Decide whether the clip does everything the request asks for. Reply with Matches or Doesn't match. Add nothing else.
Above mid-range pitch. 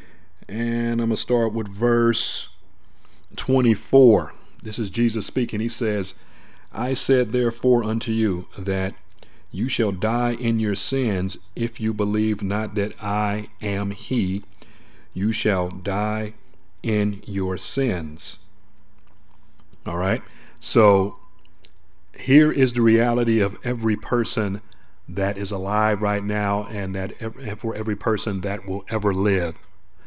Doesn't match